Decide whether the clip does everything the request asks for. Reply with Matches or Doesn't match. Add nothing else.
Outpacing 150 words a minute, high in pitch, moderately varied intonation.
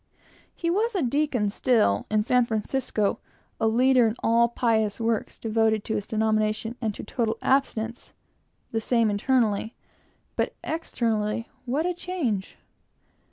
Doesn't match